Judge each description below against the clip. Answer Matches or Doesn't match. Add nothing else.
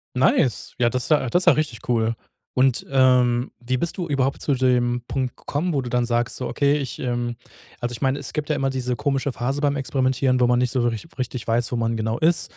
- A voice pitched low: Matches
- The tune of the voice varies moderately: Doesn't match